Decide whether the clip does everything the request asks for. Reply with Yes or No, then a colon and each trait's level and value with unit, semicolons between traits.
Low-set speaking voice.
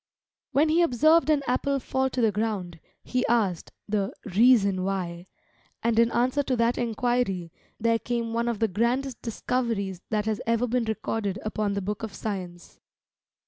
No: high, 230 Hz